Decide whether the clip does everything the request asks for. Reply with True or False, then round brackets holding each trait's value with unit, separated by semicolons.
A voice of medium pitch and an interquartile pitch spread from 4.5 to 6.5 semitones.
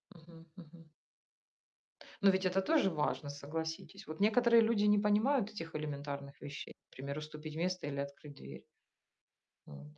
True (160 Hz; 5.6 semitones)